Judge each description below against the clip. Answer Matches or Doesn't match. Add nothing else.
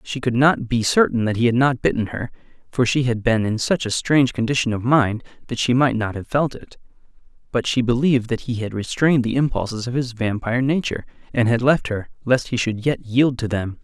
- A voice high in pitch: Doesn't match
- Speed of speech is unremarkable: Doesn't match